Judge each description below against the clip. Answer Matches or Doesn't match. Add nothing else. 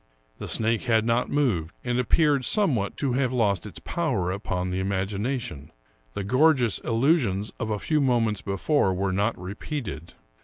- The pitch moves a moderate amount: Matches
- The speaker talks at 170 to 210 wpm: Doesn't match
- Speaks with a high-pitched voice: Doesn't match